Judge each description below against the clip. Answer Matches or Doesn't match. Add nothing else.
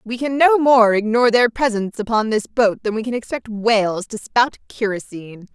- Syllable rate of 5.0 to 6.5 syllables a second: Matches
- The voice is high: Matches